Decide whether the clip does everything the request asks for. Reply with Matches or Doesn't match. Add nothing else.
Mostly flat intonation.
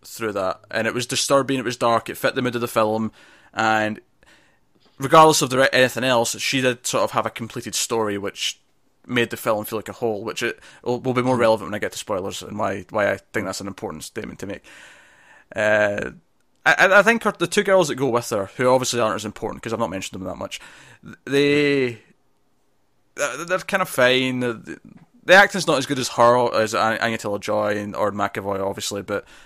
Doesn't match